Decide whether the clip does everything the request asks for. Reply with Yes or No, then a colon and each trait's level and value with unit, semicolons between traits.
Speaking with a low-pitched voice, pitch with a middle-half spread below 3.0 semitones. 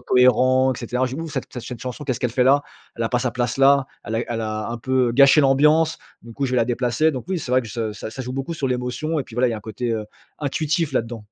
Yes: low, 125 Hz; narrow, 2.6 semitones